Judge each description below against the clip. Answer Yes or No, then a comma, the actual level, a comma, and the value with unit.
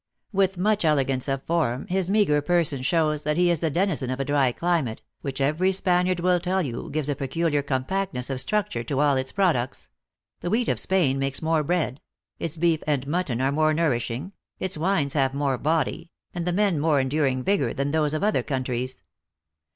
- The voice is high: No, medium, 150 Hz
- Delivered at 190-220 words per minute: Yes, average, 195 wpm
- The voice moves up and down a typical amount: Yes, average, 4.6 semitones